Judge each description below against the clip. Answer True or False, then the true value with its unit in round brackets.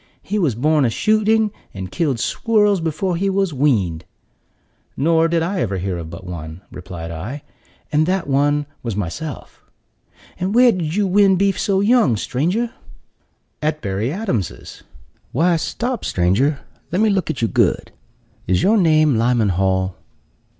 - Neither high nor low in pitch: True (155 Hz)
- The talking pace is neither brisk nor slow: True (155 wpm)